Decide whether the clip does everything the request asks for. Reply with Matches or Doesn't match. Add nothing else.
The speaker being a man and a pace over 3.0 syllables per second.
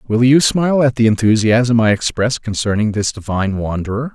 Matches